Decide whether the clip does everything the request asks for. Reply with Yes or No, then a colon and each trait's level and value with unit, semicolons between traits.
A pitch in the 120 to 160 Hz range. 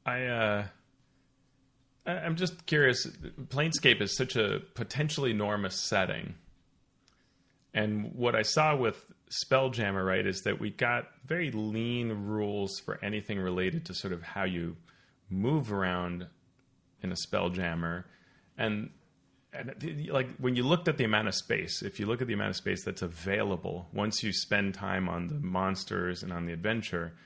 No: low, 105 Hz